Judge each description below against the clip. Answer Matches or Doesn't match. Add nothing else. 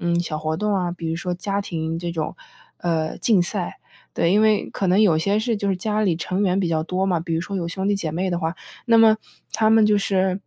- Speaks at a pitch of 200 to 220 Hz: Doesn't match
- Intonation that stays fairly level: Doesn't match